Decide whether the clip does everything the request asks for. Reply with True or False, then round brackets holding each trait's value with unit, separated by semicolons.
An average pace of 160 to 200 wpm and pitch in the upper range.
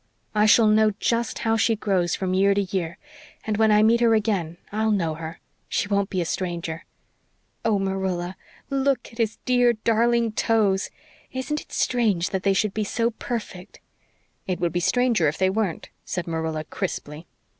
True (175 wpm; 205 Hz)